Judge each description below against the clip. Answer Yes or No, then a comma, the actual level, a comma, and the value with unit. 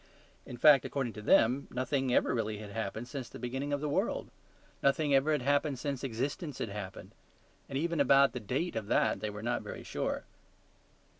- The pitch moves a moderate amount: Yes, average, 3.9 semitones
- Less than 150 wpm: No, average, 195 wpm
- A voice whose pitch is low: Yes, low, 130 Hz